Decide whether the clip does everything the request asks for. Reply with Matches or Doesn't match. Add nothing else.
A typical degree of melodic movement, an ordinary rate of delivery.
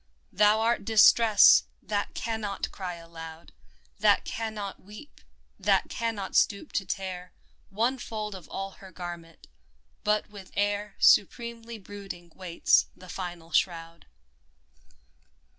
Doesn't match